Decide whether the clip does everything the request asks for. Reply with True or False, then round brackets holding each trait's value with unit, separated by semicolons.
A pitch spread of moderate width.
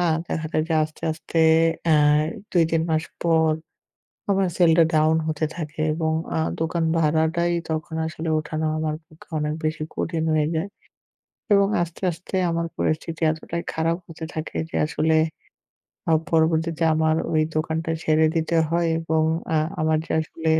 False (0.9 semitones)